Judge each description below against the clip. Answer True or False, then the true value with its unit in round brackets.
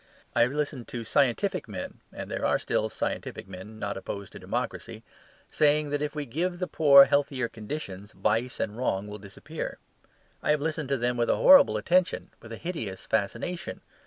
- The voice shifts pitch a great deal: True (6.0 semitones)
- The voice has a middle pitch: False (125 Hz)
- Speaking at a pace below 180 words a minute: False (185 wpm)